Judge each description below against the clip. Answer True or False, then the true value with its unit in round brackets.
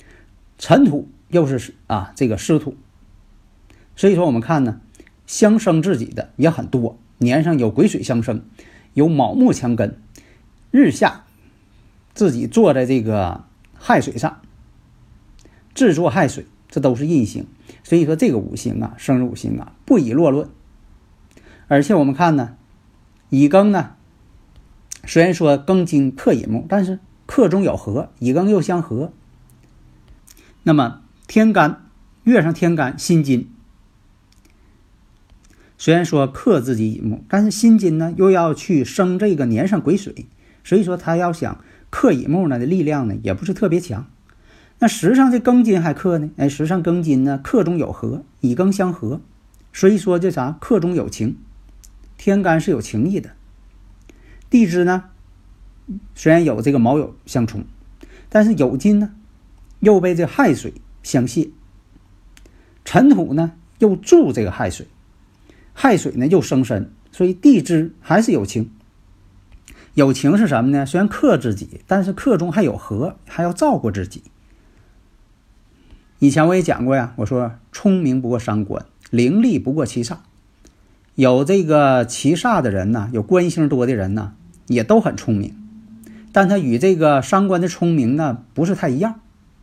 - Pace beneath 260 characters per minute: True (215 characters per minute)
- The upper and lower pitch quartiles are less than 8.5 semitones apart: False (9.0 semitones)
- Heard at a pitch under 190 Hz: True (140 Hz)